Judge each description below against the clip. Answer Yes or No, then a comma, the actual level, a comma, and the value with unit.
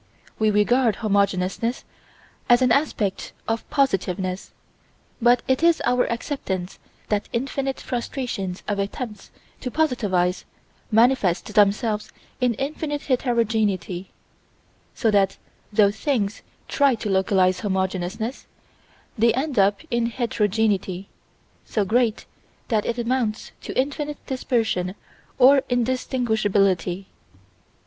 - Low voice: No, high, 220 Hz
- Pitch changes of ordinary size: Yes, average, 4.2 semitones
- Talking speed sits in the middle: No, slow, 105 wpm